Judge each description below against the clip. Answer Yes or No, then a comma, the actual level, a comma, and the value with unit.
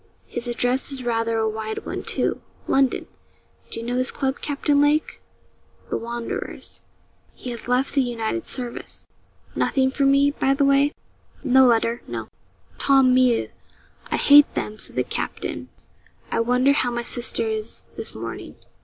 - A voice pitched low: No, very high, 255 Hz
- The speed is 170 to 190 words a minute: No, average, 155 wpm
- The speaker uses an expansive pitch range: No, average, 2.7 semitones